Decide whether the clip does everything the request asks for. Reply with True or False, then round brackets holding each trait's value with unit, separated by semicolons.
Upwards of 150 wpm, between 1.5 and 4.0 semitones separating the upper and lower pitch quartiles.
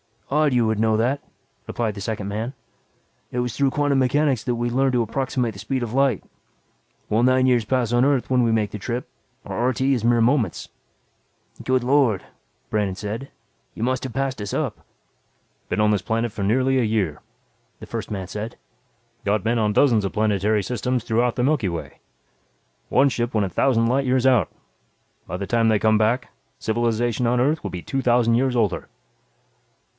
True (190 wpm; 3.2 semitones)